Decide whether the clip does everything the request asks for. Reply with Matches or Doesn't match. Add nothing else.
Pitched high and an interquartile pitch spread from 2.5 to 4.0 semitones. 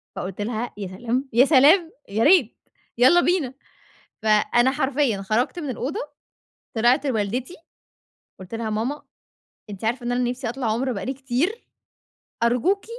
Matches